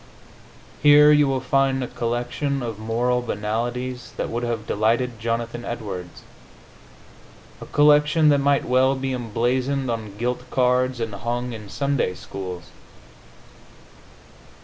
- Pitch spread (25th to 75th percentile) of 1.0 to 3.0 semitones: Yes, average, 2.7 semitones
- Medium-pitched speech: No, low, 125 Hz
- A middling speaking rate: No, slow, 125 wpm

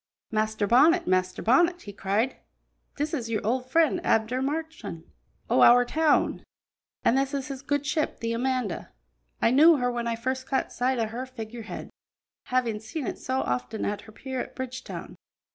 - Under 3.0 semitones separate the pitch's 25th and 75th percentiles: No, average, 3.7 semitones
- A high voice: Yes, very high, 255 Hz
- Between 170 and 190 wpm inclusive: Yes, average, 180 wpm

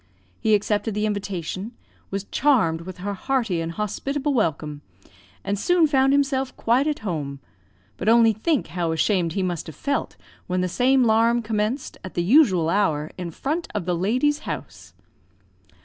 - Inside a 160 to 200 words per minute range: Yes, average, 165 wpm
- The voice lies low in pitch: No, high, 210 Hz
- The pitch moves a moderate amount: No, wide, 6.7 semitones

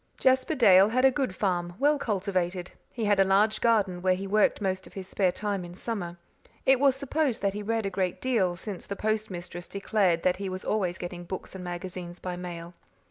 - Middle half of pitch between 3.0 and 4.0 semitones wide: Yes, average, 3.4 semitones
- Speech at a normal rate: No, fast, 210 wpm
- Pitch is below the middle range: No, high, 195 Hz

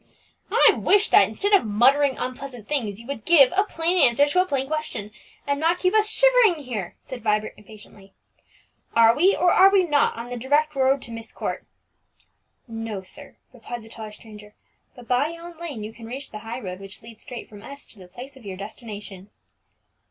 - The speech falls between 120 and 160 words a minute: No, average, 200 wpm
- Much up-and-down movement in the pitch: Yes, wide, 6.0 semitones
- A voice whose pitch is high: Yes, very high, 250 Hz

